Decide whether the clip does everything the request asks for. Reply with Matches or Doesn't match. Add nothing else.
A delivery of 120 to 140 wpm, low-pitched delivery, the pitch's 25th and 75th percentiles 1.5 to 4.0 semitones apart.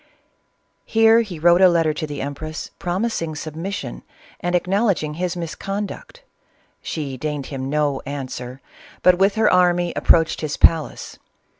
Doesn't match